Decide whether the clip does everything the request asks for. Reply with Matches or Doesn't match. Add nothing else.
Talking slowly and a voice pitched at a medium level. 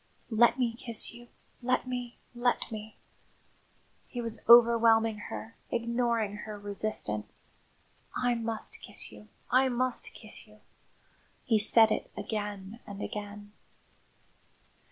Doesn't match